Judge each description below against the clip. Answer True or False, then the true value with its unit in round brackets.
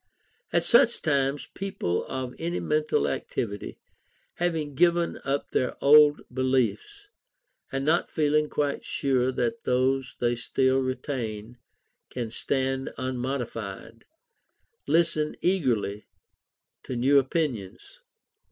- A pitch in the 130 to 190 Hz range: True (135 Hz)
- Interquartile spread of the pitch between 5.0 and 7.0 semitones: False (3.6 semitones)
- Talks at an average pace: False (105 wpm)